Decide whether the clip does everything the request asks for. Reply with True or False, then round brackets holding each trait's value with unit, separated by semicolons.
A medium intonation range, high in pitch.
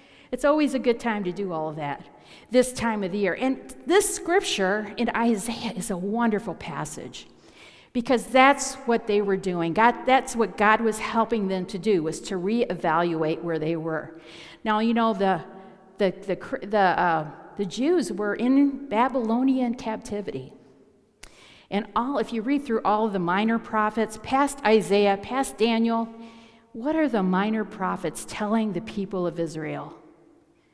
True (3.8 semitones; 215 Hz)